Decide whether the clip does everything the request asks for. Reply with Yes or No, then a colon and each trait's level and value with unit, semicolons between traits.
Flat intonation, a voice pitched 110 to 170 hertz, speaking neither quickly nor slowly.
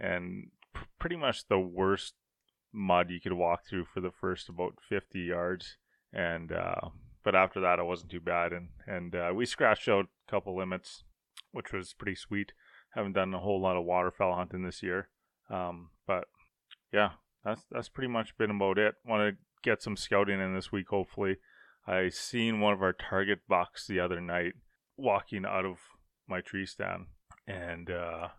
No: narrow, 2.0 semitones; very low, 95 Hz; average, 180 wpm